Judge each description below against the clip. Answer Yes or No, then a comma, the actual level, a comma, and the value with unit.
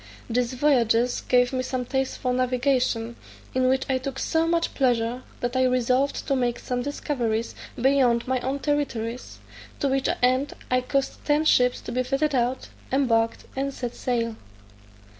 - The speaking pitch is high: Yes, very high, 255 Hz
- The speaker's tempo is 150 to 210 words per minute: Yes, average, 160 wpm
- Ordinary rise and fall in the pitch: No, narrow, 1.9 semitones